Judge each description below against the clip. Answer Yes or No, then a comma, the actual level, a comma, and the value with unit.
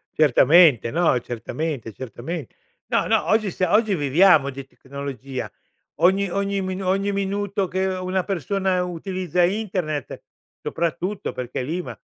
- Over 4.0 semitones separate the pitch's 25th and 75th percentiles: Yes, average, 5.3 semitones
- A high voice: No, medium, 180 Hz